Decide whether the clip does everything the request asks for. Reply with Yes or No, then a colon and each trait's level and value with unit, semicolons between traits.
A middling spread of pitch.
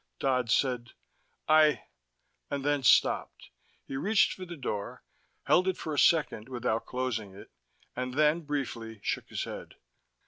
Yes: average, 4.3 semitones